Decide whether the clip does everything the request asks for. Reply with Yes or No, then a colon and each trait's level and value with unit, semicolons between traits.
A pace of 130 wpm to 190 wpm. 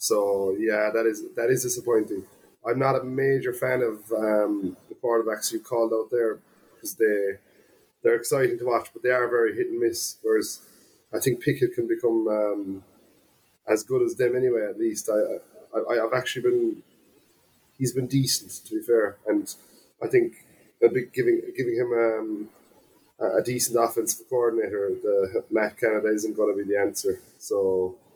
Yes: average, 170 wpm